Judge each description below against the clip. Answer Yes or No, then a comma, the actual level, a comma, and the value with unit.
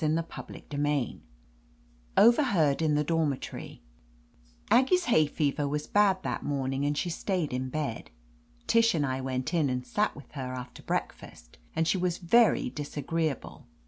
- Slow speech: No, average, 160 wpm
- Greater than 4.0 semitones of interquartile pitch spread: Yes, average, 4.4 semitones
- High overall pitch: No, medium, 150 Hz